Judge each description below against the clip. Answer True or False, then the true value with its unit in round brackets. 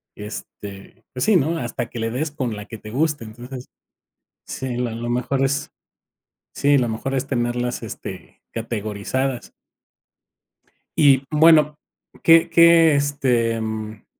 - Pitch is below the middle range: True (125 Hz)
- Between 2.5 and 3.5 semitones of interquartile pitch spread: False (3.9 semitones)